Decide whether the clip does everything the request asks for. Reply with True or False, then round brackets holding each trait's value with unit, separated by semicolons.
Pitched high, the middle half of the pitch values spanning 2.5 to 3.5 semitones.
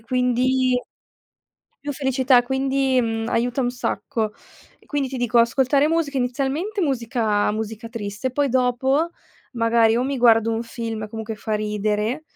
True (245 Hz; 2.9 semitones)